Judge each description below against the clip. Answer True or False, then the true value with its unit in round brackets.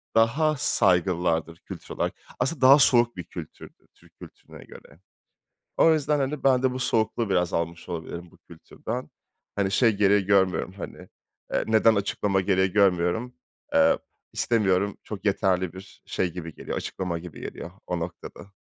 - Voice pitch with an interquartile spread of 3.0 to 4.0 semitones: False (5.0 semitones)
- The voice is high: False (100 Hz)